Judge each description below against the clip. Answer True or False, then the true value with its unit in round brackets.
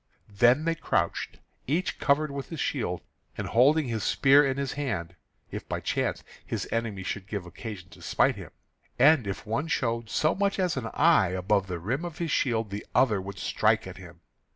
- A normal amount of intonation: False (6.7 semitones)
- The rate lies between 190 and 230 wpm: True (195 wpm)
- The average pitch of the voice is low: True (115 Hz)